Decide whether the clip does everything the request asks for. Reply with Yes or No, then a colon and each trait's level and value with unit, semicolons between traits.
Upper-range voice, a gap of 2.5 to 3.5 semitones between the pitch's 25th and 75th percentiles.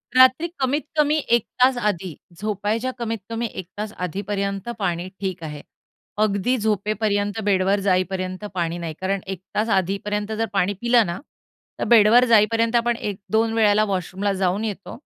Yes: high, 205 Hz; average, 3.0 semitones